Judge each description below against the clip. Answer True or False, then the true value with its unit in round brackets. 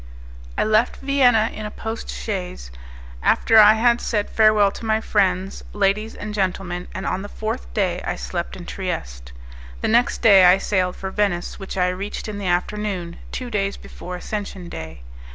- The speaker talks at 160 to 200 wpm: True (175 wpm)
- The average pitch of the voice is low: False (200 Hz)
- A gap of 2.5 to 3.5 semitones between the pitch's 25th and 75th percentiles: True (3.1 semitones)